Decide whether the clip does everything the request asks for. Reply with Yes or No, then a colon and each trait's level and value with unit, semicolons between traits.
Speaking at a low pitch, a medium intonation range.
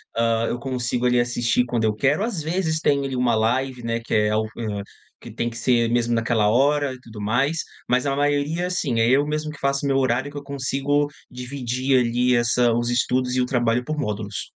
Yes: low, 125 Hz; average, 3.1 semitones